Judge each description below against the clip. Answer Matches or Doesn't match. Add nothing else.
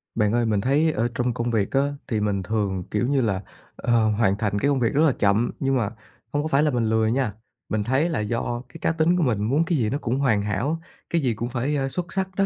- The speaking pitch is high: Doesn't match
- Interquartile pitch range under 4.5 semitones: Doesn't match